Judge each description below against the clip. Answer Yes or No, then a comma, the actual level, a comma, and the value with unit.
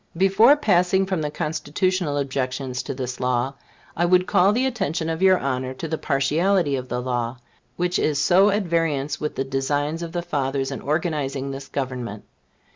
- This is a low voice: No, medium, 150 Hz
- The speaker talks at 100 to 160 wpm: No, average, 180 wpm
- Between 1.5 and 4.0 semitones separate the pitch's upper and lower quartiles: No, average, 5.0 semitones